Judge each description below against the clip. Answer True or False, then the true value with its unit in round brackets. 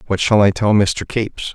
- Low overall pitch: True (100 Hz)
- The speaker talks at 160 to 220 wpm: False (235 wpm)